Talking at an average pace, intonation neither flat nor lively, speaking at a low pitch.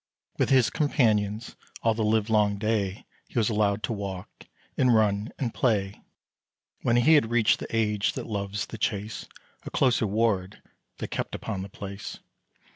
No: average, 165 wpm; narrow, 2.3 semitones; low, 110 Hz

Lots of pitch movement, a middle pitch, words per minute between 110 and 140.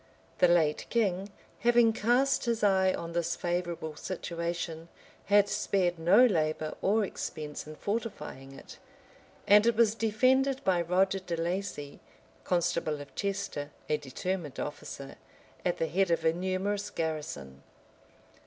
No: average, 4.2 semitones; medium, 180 Hz; slow, 135 wpm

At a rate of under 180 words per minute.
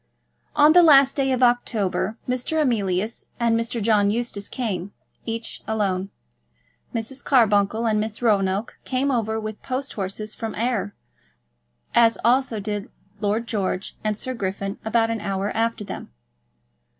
Yes: average, 140 wpm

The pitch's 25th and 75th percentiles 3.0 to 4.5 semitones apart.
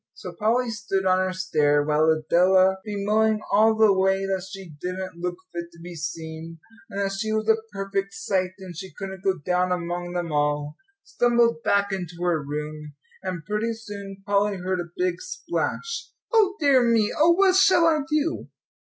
Yes: average, 3.6 semitones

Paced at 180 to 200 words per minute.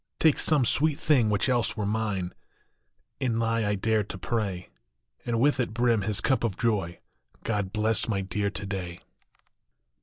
No: average, 160 wpm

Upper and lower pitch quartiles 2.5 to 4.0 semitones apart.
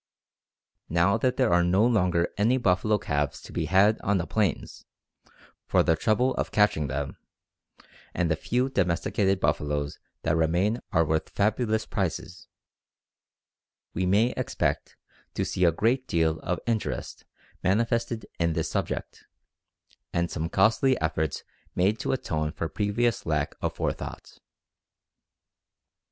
No: average, 5.1 semitones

